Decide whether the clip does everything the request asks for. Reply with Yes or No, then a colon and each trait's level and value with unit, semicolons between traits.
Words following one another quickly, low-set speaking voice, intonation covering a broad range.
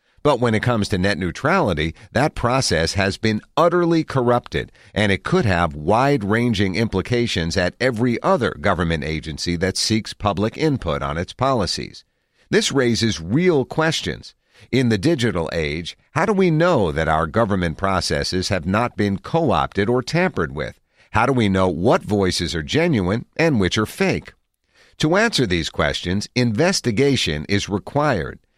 No: average, 155 wpm; low, 110 Hz; wide, 6.2 semitones